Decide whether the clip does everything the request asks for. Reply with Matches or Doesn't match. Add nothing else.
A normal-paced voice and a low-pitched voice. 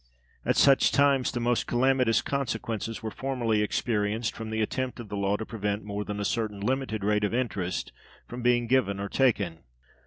Matches